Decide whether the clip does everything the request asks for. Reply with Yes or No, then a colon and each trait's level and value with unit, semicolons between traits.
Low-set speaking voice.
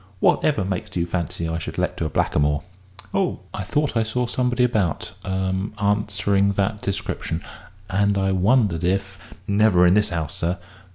Yes: low, 100 Hz